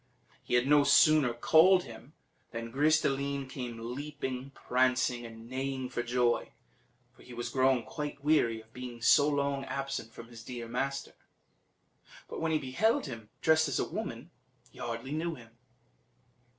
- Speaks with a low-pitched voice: Yes, low, 130 Hz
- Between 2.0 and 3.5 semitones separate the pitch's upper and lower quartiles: Yes, average, 3.0 semitones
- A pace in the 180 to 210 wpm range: No, average, 165 wpm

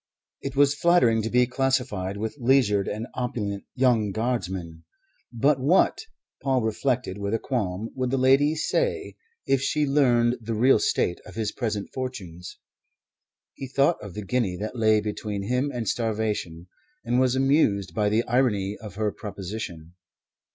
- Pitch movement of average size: Yes, average, 4.2 semitones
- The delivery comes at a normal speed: Yes, average, 160 wpm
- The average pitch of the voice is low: Yes, low, 115 Hz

